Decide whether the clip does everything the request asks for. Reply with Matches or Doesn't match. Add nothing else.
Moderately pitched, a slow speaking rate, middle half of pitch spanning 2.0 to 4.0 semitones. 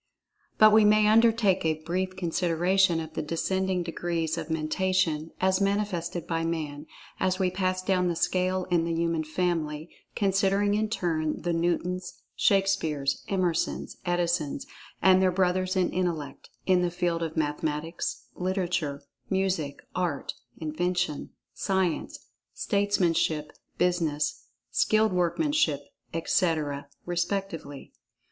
Matches